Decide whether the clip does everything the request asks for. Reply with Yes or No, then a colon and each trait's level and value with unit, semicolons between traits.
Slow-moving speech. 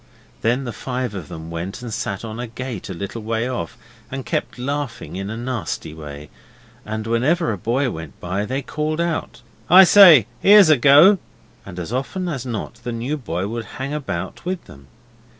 No: average, 190 wpm